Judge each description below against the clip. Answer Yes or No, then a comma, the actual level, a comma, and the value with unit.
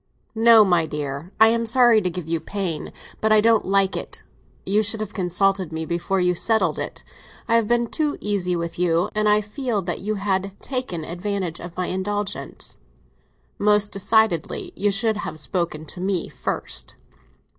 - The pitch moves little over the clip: No, average, 3.5 semitones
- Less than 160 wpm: No, average, 175 wpm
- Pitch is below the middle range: No, high, 195 Hz